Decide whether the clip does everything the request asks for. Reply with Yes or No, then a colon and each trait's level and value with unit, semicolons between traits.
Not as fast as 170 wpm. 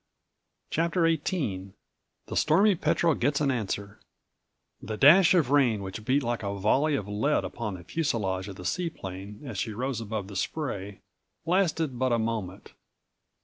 Yes: average, 155 wpm